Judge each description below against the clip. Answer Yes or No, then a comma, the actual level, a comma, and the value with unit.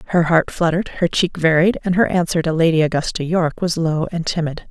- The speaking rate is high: Yes, fast, 215 wpm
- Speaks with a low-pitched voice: No, medium, 170 Hz